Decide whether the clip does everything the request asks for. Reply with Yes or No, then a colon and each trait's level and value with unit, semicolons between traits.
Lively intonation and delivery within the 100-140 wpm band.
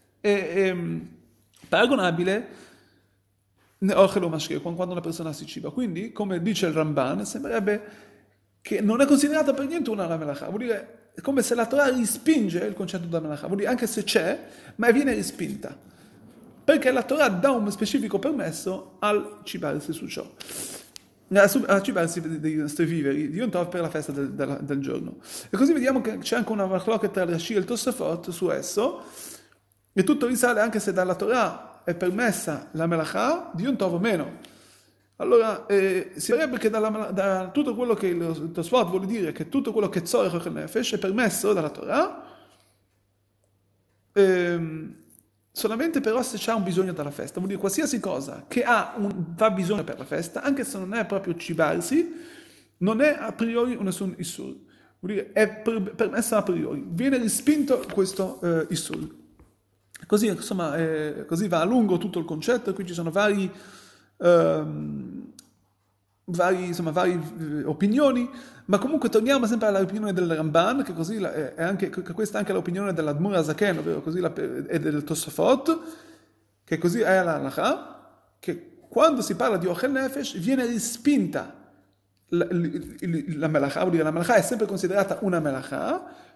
No: wide, 6.2 semitones; average, 165 wpm